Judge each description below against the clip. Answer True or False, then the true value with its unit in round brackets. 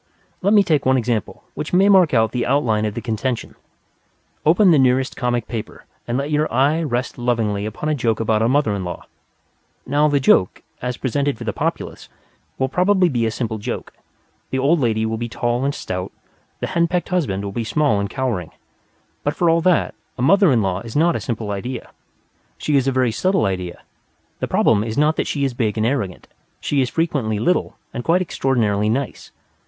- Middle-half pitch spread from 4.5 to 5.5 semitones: True (5.2 semitones)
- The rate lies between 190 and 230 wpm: True (205 wpm)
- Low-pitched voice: True (125 Hz)